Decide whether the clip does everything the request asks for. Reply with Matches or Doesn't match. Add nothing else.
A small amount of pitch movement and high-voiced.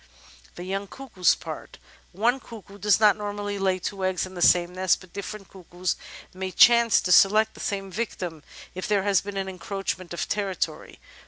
Matches